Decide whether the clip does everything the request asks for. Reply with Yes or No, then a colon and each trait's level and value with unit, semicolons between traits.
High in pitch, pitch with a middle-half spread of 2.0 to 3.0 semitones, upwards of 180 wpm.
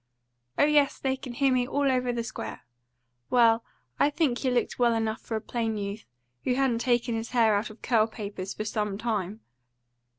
Yes: high, 235 Hz; narrow, 2.6 semitones; average, 195 wpm